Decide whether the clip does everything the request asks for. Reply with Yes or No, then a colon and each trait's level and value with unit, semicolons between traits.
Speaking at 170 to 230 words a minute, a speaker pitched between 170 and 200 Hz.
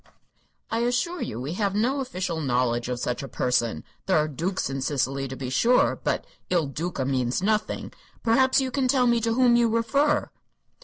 Yes: average, 190 wpm; medium, 185 Hz